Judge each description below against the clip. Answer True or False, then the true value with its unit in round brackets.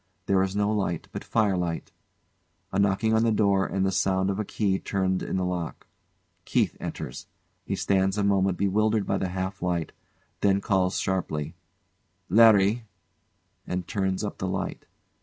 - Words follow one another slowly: False (165 wpm)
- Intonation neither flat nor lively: False (1.6 semitones)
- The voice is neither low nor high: False (95 Hz)